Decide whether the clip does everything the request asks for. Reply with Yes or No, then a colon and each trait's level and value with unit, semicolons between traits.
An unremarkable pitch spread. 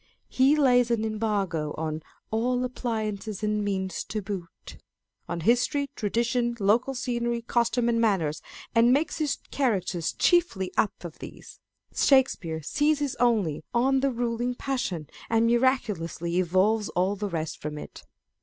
Yes: average, 4.8 semitones